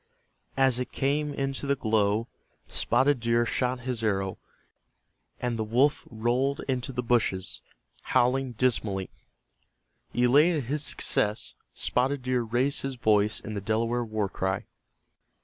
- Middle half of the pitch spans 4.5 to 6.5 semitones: No, average, 3.5 semitones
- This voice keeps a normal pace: No, slow, 130 wpm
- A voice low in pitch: Yes, low, 120 Hz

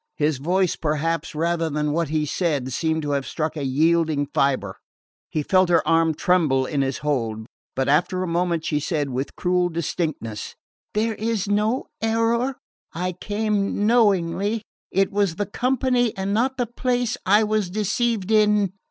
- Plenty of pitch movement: Yes, wide, 5.7 semitones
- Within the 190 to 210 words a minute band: No, average, 160 wpm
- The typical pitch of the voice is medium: Yes, medium, 175 Hz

